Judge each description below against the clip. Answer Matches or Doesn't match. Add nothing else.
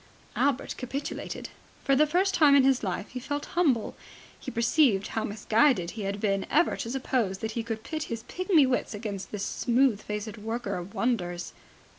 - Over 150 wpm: Matches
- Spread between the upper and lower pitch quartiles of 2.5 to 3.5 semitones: Doesn't match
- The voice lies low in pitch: Doesn't match